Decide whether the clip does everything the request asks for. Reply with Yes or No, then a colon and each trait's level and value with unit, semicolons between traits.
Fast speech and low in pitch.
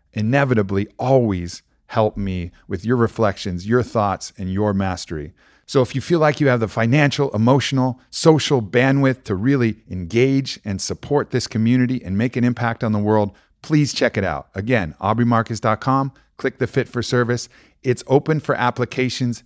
No: average, 165 wpm; low, 120 Hz